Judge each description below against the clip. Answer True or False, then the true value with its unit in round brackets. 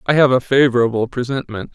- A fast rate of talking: False (170 wpm)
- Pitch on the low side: True (125 Hz)